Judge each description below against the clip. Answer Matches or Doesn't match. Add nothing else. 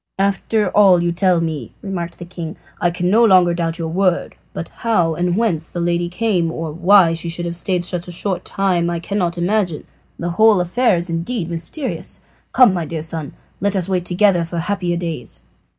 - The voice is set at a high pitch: Doesn't match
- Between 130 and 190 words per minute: Doesn't match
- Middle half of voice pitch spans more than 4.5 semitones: Doesn't match